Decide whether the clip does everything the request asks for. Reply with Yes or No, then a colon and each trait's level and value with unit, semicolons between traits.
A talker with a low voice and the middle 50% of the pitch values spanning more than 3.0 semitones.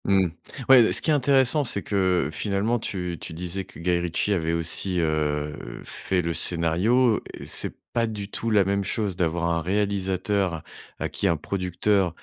Yes: very low, 95 Hz; average, 3.5 semitones